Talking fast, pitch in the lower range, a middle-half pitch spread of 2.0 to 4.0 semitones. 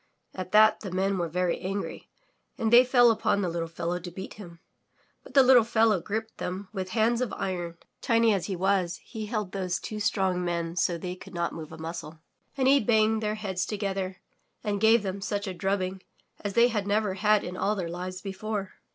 No: fast, 210 wpm; high, 195 Hz; average, 3.1 semitones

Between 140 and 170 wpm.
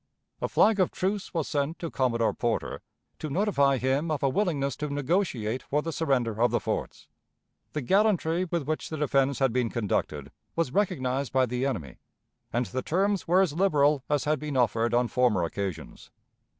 No: average, 180 wpm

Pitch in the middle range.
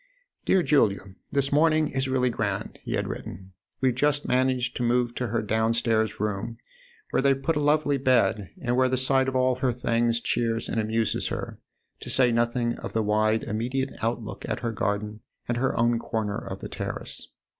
No: low, 120 Hz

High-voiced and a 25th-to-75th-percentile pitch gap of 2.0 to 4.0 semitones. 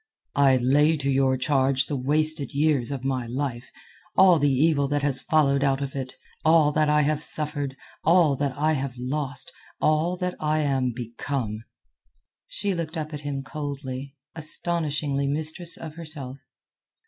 No: medium, 145 Hz; narrow, 2.4 semitones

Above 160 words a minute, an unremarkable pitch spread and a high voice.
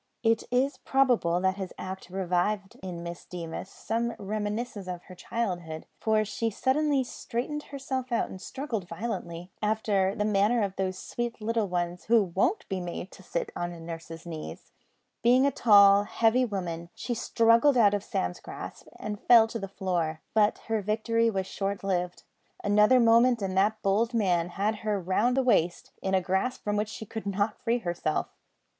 Yes: average, 175 wpm; average, 3.9 semitones; high, 205 Hz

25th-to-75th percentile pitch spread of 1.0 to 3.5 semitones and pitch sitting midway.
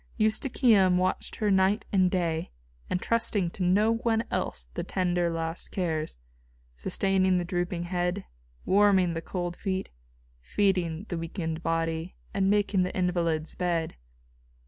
Yes: average, 2.7 semitones; medium, 180 Hz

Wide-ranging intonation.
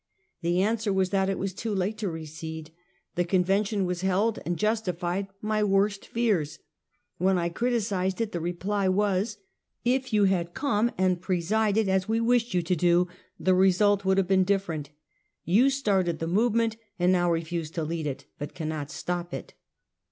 No: average, 3.2 semitones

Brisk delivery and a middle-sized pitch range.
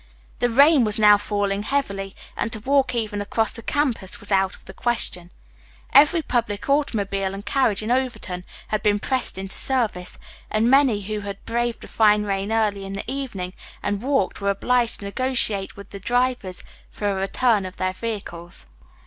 No: average, 180 wpm; average, 3.8 semitones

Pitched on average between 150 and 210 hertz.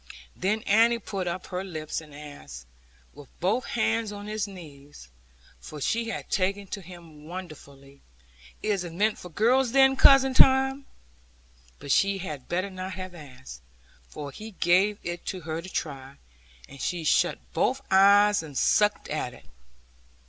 Yes: medium, 185 Hz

